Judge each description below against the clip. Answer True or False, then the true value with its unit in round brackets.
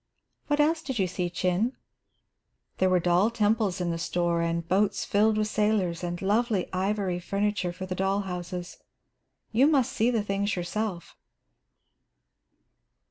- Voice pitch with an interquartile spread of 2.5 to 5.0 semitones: True (3.3 semitones)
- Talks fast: False (145 wpm)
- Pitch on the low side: False (195 Hz)